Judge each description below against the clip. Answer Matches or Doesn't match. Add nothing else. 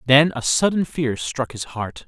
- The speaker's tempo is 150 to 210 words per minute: Matches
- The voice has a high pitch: Doesn't match